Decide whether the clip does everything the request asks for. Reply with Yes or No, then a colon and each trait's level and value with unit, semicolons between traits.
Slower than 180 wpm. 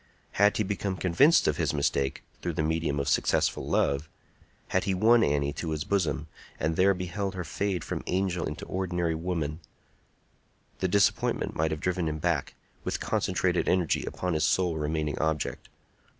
Yes: average, 160 wpm